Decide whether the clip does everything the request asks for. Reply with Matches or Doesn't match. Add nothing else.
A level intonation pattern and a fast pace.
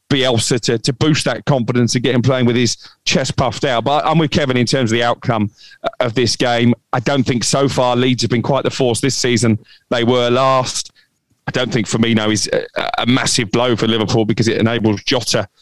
Matches